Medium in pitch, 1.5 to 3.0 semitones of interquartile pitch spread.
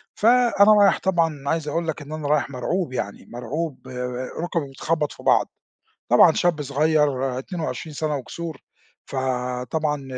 No: medium, 150 Hz; average, 3.8 semitones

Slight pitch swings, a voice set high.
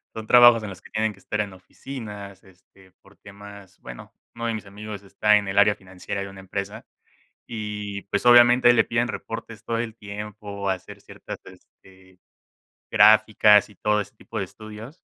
No: narrow, 2.1 semitones; low, 105 Hz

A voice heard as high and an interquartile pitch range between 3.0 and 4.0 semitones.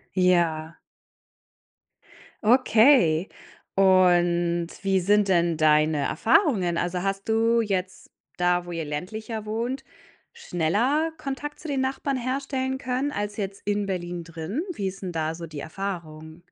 No: high, 195 Hz; wide, 5.4 semitones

